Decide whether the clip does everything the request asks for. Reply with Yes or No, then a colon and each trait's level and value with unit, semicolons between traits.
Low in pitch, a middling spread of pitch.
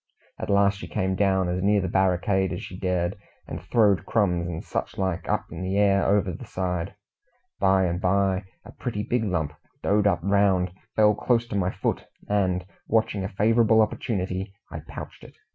No: very low, 95 Hz; narrow, 2.1 semitones